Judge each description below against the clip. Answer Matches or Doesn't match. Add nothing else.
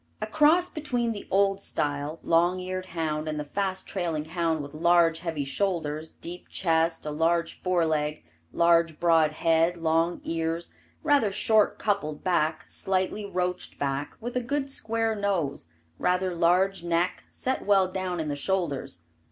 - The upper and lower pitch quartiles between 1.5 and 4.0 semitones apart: Matches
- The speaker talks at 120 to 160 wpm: Matches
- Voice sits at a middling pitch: Matches